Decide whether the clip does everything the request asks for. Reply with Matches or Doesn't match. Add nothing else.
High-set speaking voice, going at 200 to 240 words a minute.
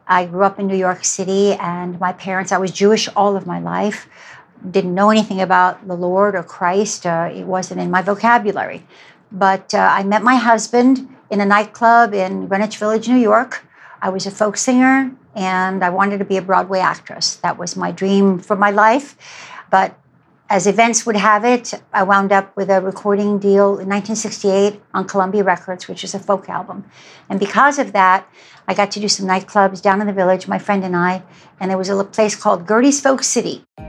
Matches